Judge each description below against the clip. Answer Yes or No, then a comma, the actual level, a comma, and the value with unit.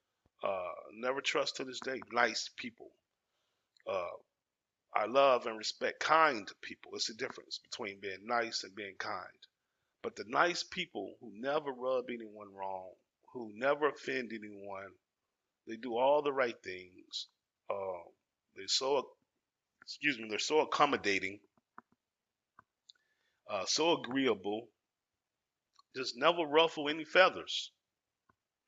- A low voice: Yes, low, 120 Hz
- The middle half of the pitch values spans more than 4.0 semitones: Yes, average, 4.7 semitones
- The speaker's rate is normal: No, slow, 125 wpm